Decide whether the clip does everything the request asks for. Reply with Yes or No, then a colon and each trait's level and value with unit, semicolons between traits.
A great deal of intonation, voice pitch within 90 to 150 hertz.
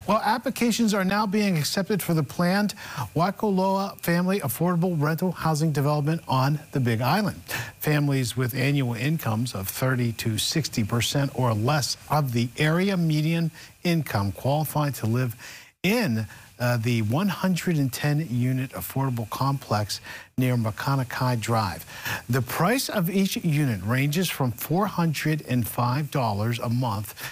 Yes: wide, 5.9 semitones; medium, 140 Hz